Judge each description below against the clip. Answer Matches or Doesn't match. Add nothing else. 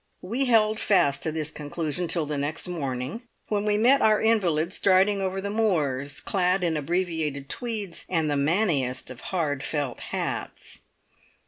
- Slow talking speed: Doesn't match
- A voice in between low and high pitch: Matches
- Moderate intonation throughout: Doesn't match